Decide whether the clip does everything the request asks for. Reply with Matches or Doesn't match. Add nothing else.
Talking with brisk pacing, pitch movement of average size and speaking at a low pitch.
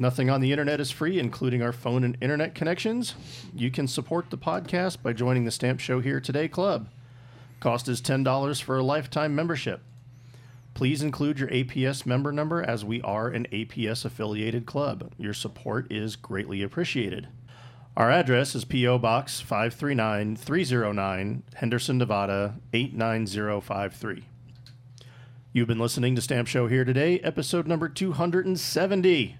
Doesn't match